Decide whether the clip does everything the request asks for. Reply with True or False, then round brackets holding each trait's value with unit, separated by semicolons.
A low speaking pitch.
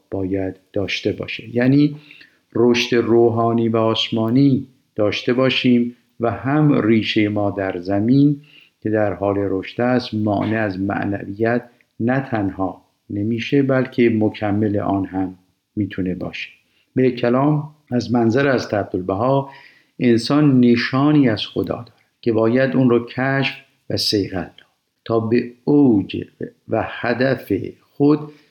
True (115 Hz)